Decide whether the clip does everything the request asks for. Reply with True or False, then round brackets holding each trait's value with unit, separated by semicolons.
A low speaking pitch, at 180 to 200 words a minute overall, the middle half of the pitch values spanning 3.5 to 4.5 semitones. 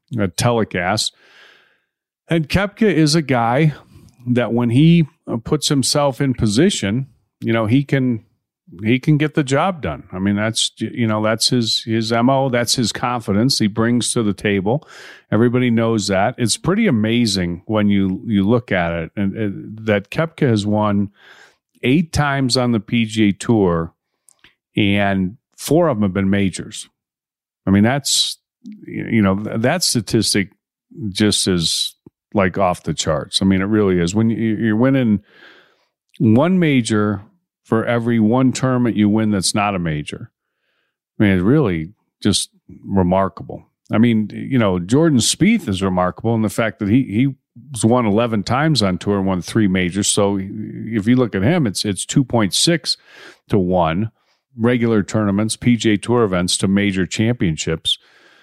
False (110 Hz; 160 wpm; 3.9 semitones)